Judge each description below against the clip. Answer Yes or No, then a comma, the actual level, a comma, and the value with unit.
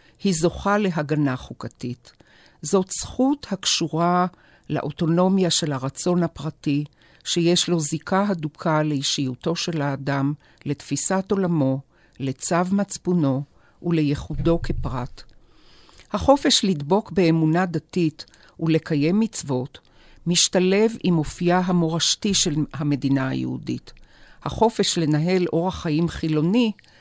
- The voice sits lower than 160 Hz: No, medium, 165 Hz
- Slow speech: Yes, slow, 95 wpm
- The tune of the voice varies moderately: Yes, average, 4.0 semitones